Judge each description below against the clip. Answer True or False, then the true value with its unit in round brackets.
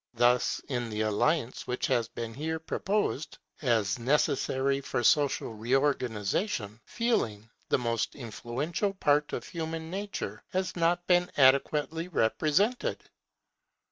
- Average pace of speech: False (115 wpm)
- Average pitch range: False (5.9 semitones)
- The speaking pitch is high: False (140 Hz)